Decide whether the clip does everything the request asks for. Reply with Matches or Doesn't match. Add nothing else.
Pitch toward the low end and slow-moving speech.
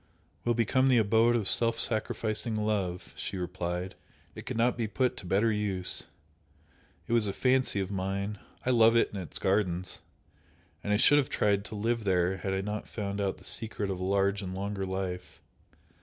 Doesn't match